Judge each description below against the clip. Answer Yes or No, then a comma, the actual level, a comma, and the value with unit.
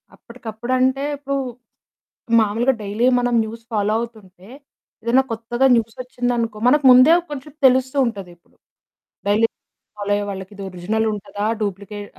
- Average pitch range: Yes, average, 3.6 semitones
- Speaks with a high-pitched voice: Yes, high, 225 Hz